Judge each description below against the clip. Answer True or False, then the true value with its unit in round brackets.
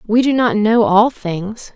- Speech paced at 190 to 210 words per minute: True (205 wpm)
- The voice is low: False (215 Hz)